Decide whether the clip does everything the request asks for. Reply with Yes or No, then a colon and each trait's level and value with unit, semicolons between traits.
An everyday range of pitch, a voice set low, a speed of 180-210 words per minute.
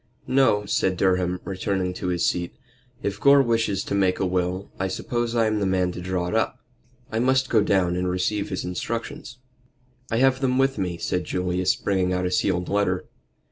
Yes: average, 3.7 semitones; very low, 95 Hz; average, 195 wpm